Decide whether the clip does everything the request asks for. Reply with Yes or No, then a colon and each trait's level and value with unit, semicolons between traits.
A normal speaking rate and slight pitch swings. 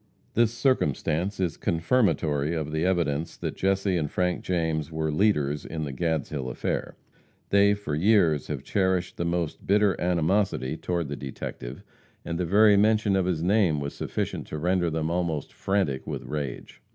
No: average, 165 wpm; average, 4.2 semitones